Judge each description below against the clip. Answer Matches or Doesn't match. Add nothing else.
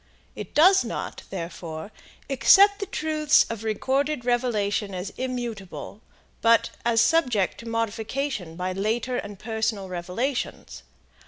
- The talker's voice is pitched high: Matches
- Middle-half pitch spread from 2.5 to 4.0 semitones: Doesn't match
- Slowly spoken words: Matches